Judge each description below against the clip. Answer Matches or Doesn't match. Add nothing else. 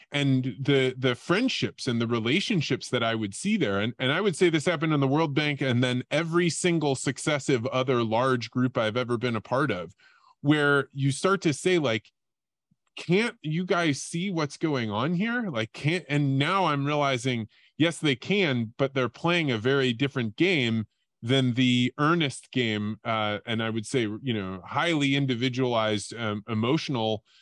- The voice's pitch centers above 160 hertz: Doesn't match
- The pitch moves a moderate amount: Matches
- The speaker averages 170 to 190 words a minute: Matches